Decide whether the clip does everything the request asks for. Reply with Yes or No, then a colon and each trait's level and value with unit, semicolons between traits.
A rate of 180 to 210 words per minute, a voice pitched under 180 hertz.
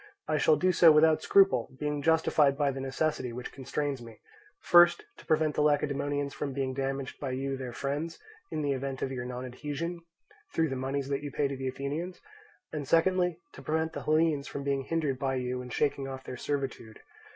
Yes: average, 195 wpm; medium, 140 Hz